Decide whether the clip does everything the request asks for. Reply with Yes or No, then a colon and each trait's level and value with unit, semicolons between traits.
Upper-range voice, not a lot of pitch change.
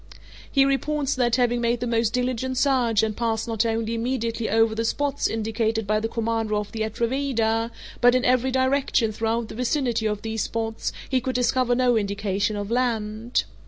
Yes: high, 230 Hz; narrow, 2.2 semitones